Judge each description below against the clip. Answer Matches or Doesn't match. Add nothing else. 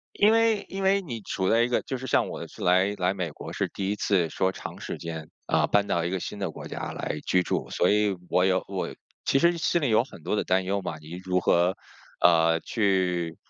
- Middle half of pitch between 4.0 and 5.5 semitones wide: Matches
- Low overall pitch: Matches